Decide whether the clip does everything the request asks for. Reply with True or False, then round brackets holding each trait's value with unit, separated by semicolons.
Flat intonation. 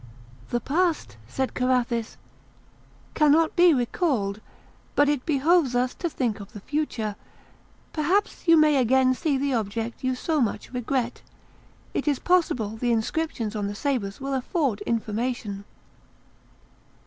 False (5.1 semitones)